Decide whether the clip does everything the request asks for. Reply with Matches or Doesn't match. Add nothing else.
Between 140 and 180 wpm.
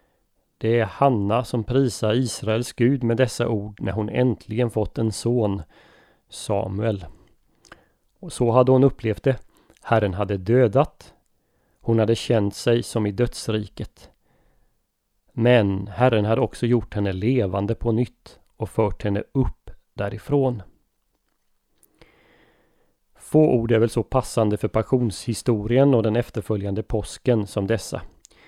Doesn't match